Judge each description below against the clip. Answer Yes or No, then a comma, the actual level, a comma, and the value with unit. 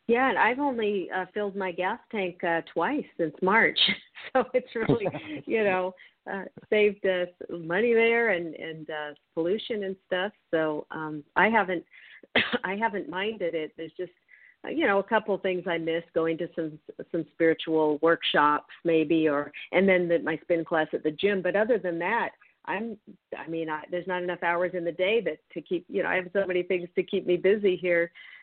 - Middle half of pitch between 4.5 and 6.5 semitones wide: No, average, 3.5 semitones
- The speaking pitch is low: No, medium, 180 Hz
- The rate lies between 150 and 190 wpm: No, average, 200 wpm